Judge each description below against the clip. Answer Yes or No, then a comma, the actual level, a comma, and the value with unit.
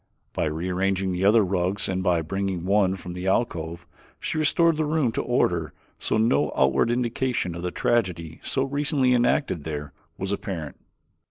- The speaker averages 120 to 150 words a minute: No, average, 165 wpm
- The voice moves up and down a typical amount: No, wide, 5.7 semitones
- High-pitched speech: No, very low, 95 Hz